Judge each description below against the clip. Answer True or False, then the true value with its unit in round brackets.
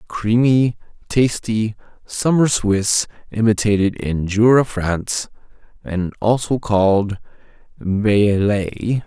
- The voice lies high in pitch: False (110 Hz)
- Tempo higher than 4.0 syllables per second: False (3.5 syllables/s)